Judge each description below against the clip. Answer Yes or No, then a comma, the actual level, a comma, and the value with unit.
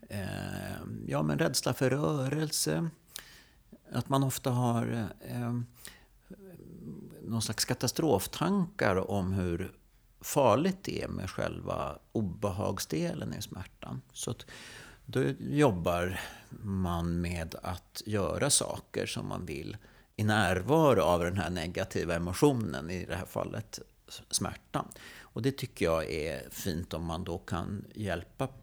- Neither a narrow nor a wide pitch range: No, wide, 6.1 semitones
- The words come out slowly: Yes, slow, 120 wpm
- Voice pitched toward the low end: Yes, low, 105 Hz